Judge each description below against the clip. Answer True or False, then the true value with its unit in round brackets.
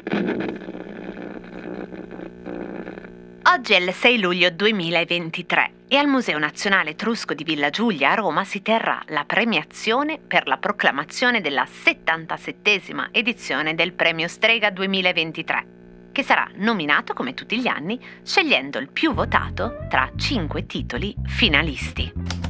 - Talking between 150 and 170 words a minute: False (120 wpm)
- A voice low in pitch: False (170 Hz)